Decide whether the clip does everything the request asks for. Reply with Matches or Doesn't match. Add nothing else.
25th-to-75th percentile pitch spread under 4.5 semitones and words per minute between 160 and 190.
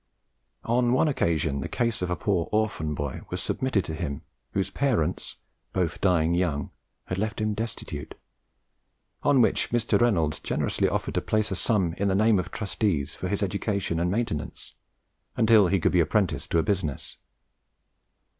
Doesn't match